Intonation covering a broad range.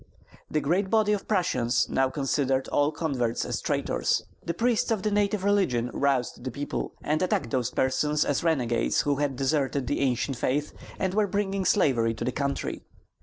Yes: wide, 6.5 semitones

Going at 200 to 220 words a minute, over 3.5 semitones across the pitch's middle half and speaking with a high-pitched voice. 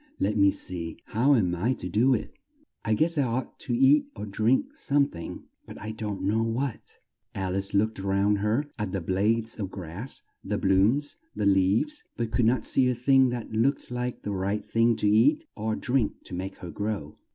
No: fast, 205 wpm; average, 4.4 semitones; low, 110 Hz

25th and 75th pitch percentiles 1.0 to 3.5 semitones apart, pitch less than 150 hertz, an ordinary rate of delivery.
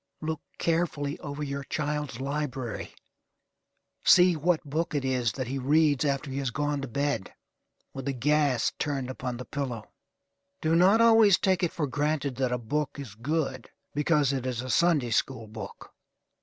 Yes: average, 2.9 semitones; medium, 140 Hz; average, 170 wpm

